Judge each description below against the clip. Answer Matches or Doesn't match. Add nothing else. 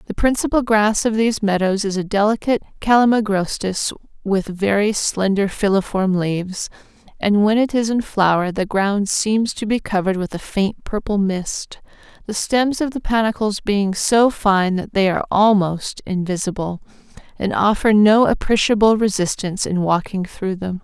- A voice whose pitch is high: Matches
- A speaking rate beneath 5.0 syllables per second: Matches